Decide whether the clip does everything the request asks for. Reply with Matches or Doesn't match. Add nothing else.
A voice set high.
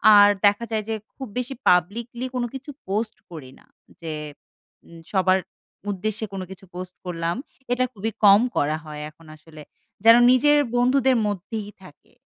Matches